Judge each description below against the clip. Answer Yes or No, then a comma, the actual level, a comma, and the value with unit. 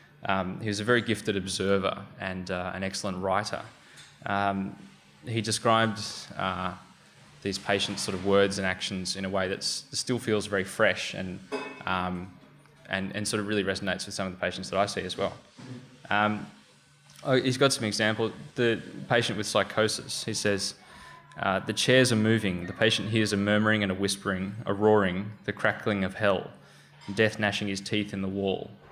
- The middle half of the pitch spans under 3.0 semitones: Yes, narrow, 2.4 semitones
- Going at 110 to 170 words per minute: No, average, 180 wpm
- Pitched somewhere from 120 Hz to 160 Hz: No, low, 100 Hz